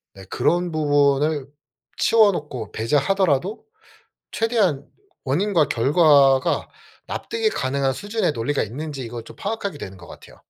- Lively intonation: Yes, wide, 6.4 semitones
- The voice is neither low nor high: Yes, medium, 145 Hz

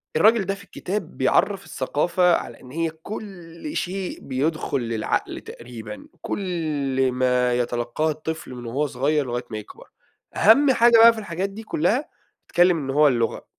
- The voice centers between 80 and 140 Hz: No, medium, 155 Hz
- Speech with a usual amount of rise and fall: No, wide, 7.1 semitones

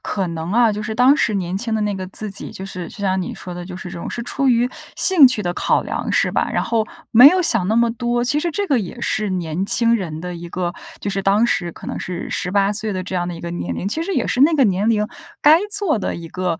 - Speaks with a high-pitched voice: Yes, high, 205 Hz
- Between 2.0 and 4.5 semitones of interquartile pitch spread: No, average, 4.9 semitones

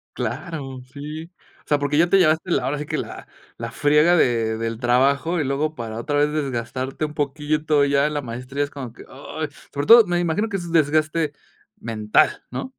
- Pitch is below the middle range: No, medium, 145 Hz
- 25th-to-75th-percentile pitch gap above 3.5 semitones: No, average, 2.9 semitones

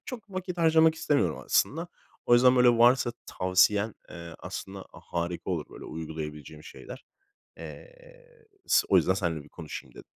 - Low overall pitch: Yes, low, 115 Hz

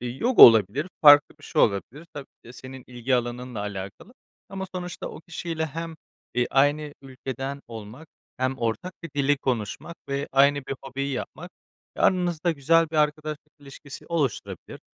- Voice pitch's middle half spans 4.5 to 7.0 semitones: No, average, 4.1 semitones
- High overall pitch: No, medium, 140 Hz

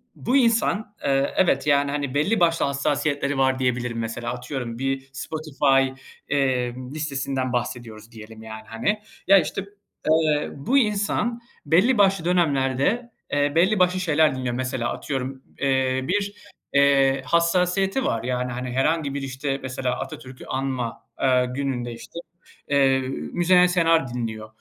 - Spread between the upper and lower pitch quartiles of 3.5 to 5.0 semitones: Yes, average, 4.7 semitones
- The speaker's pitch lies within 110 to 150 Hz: Yes, medium, 140 Hz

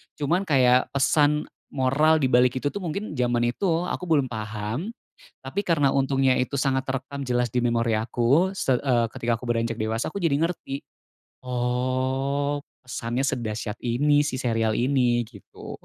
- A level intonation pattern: No, average, 3.3 semitones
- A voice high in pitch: No, low, 130 Hz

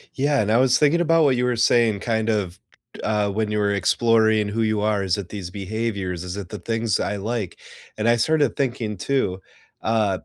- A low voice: Yes, low, 110 Hz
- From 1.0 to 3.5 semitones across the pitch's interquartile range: Yes, average, 2.8 semitones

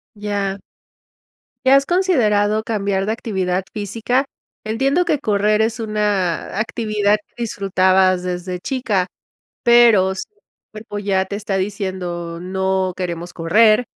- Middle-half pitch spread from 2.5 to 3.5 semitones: Yes, average, 2.8 semitones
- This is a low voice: No, high, 205 Hz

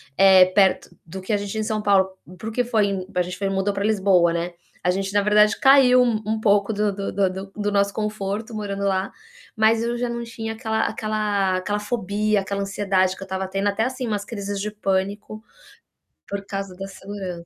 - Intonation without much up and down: Yes, narrow, 1.9 semitones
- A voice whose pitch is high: Yes, high, 200 Hz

